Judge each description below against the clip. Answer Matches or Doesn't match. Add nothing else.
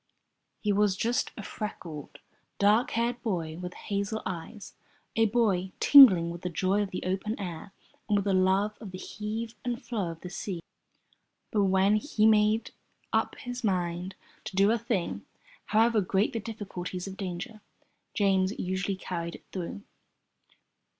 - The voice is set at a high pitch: Matches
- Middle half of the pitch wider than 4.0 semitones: Doesn't match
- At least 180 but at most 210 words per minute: Doesn't match